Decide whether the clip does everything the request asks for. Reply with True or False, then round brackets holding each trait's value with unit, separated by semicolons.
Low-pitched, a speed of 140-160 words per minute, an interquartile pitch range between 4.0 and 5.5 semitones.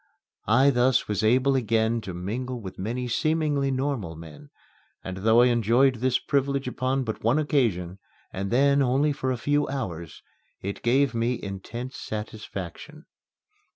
True (125 Hz; 150 wpm; 4.3 semitones)